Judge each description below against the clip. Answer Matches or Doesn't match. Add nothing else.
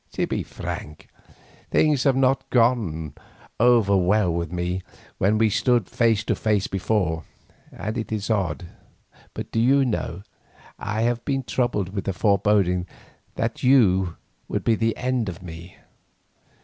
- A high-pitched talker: Doesn't match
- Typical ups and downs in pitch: Matches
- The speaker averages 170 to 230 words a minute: Doesn't match